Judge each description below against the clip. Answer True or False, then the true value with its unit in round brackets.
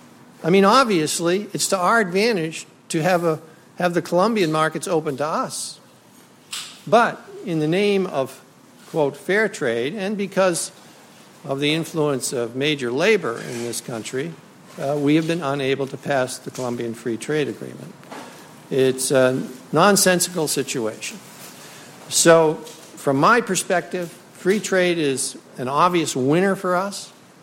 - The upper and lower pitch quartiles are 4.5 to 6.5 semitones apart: True (5.2 semitones)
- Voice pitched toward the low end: False (160 Hz)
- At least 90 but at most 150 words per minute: True (140 wpm)